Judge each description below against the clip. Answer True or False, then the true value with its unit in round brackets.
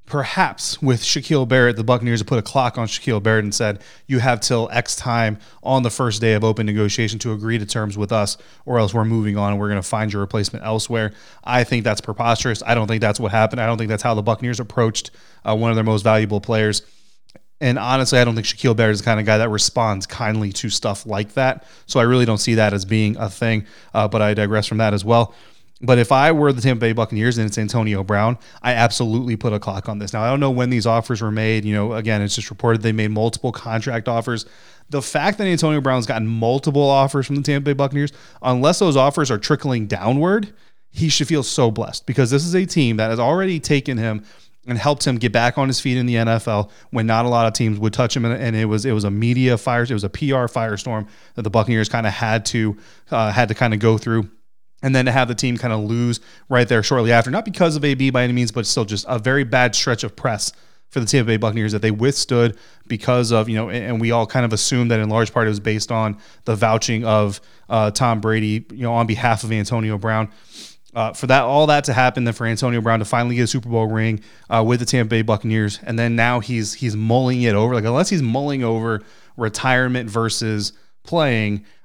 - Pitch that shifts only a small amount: True (2.3 semitones)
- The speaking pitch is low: True (115 Hz)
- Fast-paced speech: True (245 wpm)